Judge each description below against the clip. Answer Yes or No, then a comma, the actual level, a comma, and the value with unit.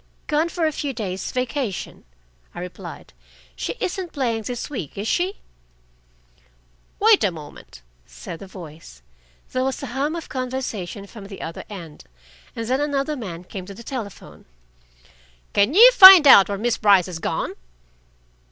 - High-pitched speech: Yes, high, 235 Hz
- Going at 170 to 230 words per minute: No, average, 155 wpm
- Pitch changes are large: Yes, wide, 7.1 semitones